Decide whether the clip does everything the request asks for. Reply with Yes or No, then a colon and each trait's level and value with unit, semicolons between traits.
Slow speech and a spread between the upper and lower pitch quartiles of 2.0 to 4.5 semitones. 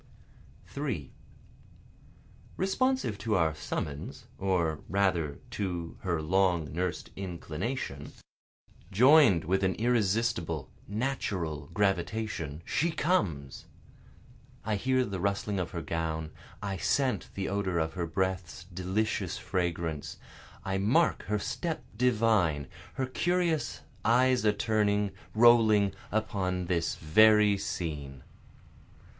No: slow, 105 wpm; average, 5.1 semitones